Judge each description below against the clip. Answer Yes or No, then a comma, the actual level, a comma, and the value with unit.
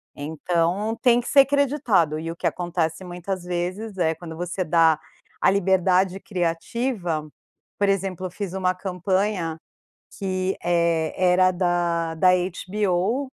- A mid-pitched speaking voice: Yes, medium, 180 Hz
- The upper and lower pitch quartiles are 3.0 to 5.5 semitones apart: No, narrow, 2.6 semitones